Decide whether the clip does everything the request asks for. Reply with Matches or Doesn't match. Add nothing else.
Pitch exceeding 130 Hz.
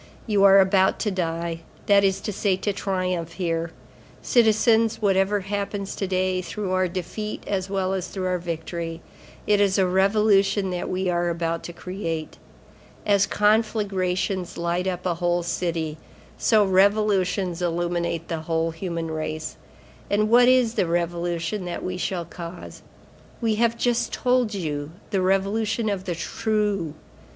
Matches